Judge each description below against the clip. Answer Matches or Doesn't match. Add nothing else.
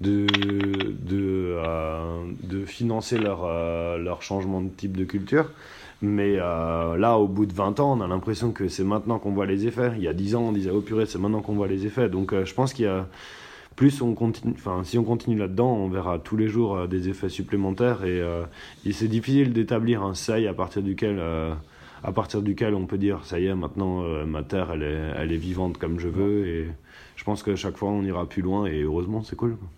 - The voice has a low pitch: Matches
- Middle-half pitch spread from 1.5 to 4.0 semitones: Matches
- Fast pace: Matches